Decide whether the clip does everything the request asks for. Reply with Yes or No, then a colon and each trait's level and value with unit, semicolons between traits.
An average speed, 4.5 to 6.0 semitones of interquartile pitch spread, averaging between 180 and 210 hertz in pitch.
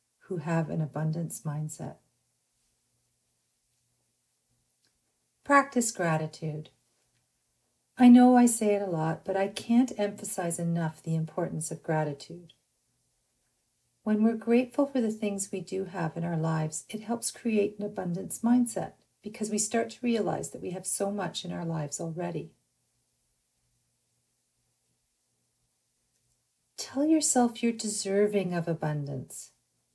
No: slow, 120 wpm; wide, 5.5 semitones; medium, 185 Hz